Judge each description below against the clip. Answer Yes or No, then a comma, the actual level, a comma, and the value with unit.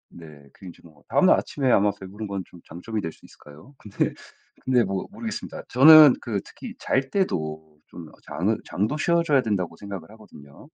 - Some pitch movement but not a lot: No, wide, 7.8 semitones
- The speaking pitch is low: Yes, low, 100 Hz